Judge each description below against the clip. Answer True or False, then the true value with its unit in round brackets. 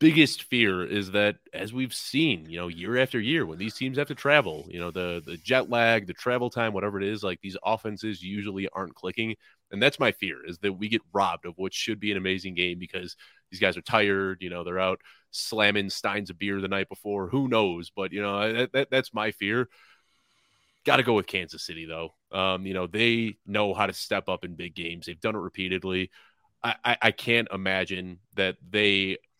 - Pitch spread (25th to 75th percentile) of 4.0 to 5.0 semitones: False (3.4 semitones)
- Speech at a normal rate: False (220 wpm)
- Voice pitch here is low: True (100 Hz)